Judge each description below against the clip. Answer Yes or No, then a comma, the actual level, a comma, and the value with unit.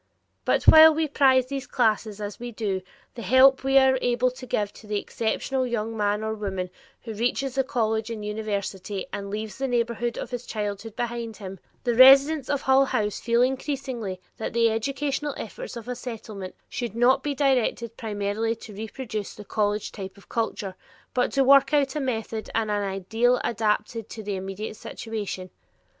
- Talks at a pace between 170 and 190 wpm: Yes, average, 180 wpm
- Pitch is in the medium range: No, high, 230 Hz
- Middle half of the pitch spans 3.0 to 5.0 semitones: Yes, average, 3.7 semitones